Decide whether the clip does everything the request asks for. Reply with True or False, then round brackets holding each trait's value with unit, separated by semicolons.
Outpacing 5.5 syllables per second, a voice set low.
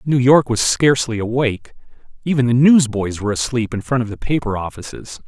True (5.9 syllables/s; 120 Hz)